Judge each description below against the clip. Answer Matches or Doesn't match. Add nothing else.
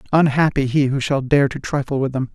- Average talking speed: Doesn't match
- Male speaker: Matches